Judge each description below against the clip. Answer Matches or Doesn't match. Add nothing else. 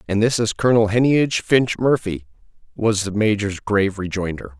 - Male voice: Matches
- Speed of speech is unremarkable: Matches